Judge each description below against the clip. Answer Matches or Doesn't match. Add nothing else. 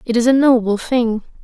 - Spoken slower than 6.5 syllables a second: Matches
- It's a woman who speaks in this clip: Matches